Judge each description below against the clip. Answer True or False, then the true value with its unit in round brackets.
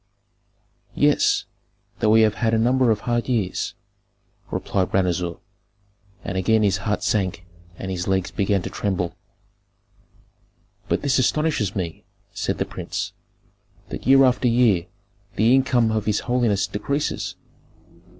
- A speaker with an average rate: False (130 wpm)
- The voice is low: True (105 Hz)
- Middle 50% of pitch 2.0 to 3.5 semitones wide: False (4.2 semitones)